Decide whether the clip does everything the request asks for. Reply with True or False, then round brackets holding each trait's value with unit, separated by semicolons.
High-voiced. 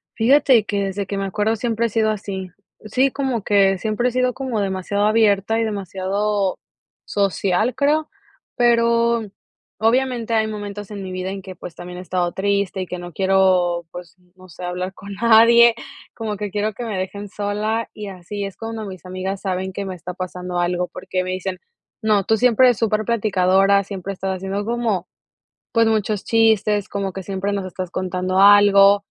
True (200 Hz)